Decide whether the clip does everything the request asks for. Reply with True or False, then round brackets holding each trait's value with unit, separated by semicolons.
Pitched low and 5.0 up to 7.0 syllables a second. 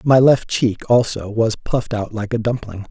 False (115 Hz; 4.6 syllables/s)